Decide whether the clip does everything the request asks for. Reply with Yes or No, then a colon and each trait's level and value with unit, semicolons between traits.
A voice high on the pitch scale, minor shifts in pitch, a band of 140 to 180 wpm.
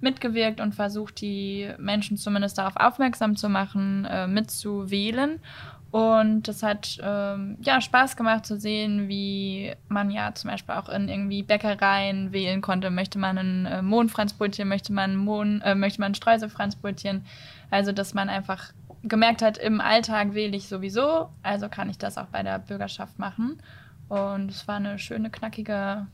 Yes: high, 205 Hz; narrow, 1.6 semitones; average, 160 wpm